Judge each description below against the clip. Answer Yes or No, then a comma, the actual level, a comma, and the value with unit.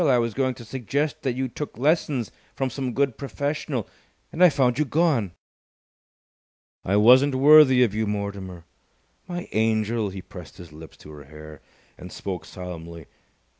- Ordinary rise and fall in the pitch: No, wide, 6.6 semitones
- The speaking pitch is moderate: No, low, 120 Hz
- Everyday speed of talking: Yes, average, 160 wpm